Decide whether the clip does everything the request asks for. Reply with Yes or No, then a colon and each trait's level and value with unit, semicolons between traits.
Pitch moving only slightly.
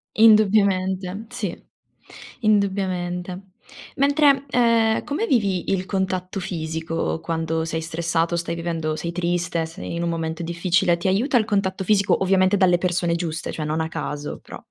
No: average, 3.2 semitones